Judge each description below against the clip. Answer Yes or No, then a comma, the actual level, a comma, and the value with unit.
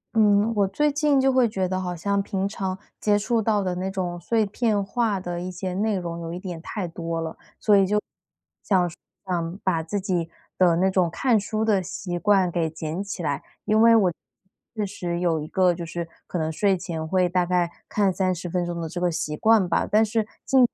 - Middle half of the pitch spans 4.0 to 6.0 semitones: No, average, 3.0 semitones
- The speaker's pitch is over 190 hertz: No, medium, 185 Hz